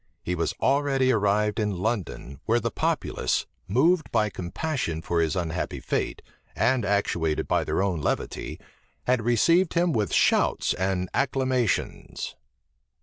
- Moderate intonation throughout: No, wide, 6.2 semitones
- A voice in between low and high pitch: No, low, 105 Hz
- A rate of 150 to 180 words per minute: No, slow, 135 wpm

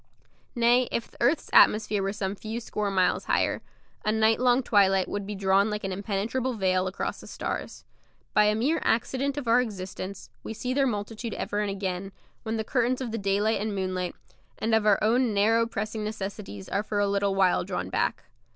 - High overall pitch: Yes, high, 210 Hz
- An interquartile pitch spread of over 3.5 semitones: No, average, 2.7 semitones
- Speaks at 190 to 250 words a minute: Yes, average, 195 wpm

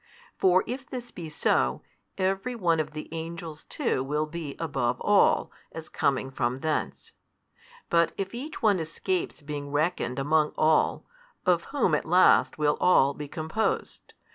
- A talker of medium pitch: Yes, medium, 160 Hz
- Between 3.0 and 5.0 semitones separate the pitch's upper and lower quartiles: Yes, average, 4.2 semitones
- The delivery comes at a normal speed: Yes, average, 150 wpm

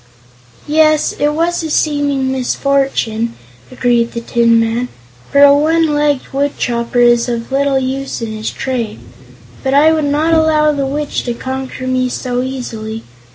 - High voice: Yes, very high, 265 Hz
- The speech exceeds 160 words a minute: No, average, 155 wpm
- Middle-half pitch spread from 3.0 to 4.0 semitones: Yes, average, 3.5 semitones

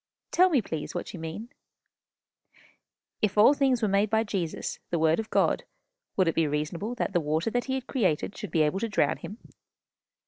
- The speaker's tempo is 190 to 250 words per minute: Yes, average, 200 wpm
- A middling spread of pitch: No, wide, 5.7 semitones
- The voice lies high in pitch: Yes, high, 200 Hz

